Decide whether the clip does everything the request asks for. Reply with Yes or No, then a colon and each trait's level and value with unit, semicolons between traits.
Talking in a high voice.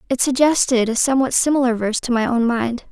Yes: very high, 250 Hz